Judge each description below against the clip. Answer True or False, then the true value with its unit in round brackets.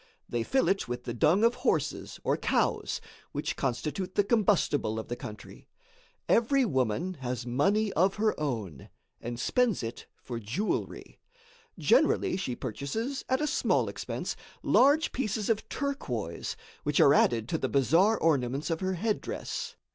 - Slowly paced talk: False (150 wpm)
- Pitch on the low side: False (165 Hz)